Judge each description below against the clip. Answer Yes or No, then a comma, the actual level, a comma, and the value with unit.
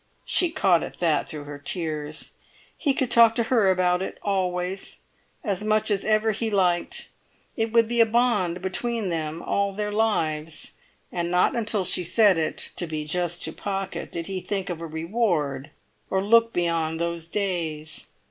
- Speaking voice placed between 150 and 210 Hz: Yes, medium, 185 Hz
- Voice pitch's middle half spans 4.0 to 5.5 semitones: Yes, average, 4.3 semitones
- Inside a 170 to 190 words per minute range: Yes, average, 175 wpm